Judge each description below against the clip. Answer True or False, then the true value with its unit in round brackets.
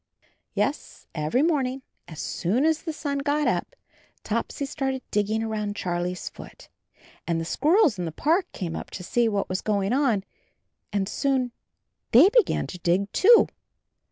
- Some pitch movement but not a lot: False (7.0 semitones)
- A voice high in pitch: True (230 Hz)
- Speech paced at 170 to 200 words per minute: False (160 wpm)